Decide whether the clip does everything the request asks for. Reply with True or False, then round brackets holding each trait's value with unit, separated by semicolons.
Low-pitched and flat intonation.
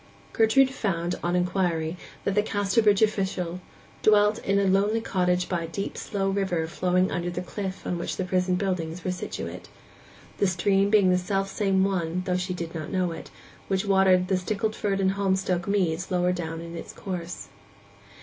False (185 Hz; 1.9 semitones)